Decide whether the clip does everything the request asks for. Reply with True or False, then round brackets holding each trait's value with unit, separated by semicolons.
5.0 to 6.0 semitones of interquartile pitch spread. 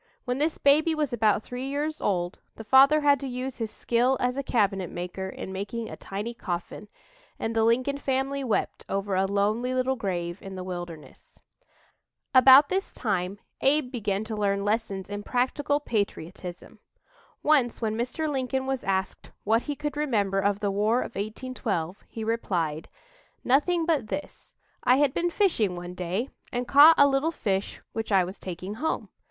True (5.5 semitones)